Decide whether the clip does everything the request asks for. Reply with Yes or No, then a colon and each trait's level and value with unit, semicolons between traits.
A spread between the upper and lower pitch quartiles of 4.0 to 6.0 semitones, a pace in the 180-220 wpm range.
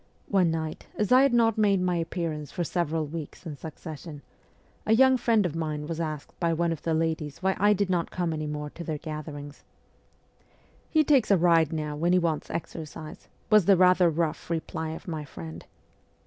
No: average, 3.0 semitones; average, 200 wpm